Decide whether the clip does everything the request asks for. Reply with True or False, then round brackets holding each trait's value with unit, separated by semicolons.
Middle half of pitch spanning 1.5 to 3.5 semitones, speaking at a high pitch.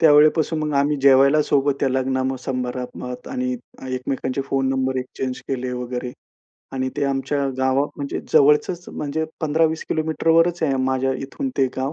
False (2.5 semitones; 135 Hz)